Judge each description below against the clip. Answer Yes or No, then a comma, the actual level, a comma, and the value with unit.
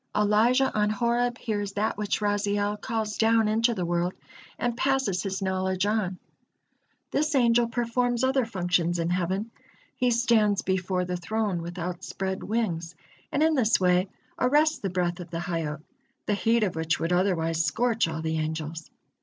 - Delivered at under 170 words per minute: Yes, average, 160 wpm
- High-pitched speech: Yes, high, 205 Hz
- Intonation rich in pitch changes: No, average, 4.5 semitones